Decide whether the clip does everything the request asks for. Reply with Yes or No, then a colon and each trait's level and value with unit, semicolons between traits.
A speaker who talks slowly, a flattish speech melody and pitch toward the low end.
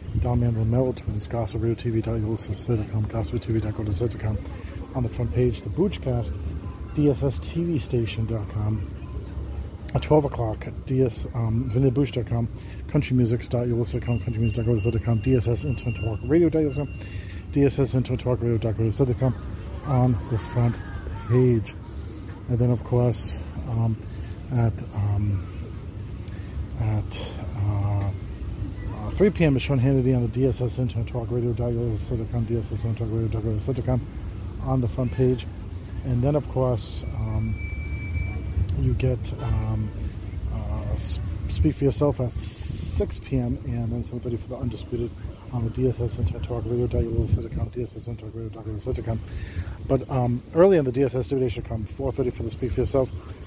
No: slow, 115 wpm; average, 3.8 semitones; low, 115 Hz